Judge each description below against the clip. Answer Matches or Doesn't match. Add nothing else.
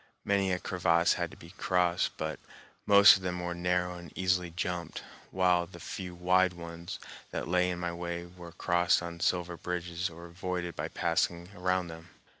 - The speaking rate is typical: Matches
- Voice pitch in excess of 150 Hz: Doesn't match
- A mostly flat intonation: Matches